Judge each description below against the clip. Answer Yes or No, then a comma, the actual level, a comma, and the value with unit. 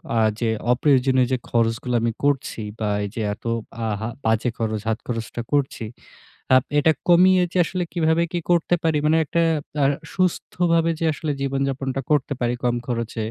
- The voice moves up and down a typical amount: No, wide, 5.7 semitones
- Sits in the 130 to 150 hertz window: Yes, low, 135 Hz